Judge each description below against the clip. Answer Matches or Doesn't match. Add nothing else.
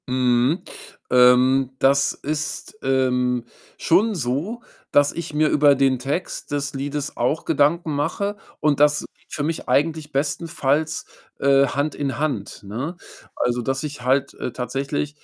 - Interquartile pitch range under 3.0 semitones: Matches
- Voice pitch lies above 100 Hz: Matches